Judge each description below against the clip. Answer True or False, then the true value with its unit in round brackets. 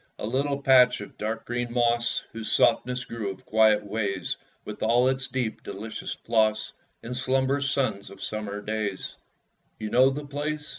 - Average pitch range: True (3.5 semitones)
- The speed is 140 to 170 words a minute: True (160 wpm)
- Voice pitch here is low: True (120 Hz)